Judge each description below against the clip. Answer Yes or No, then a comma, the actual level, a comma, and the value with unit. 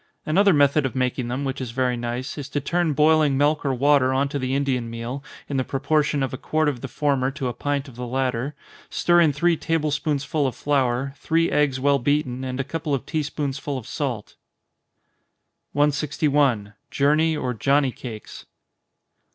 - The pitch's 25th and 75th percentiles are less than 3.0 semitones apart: Yes, narrow, 2.5 semitones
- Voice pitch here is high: No, medium, 140 Hz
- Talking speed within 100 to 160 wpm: No, average, 185 wpm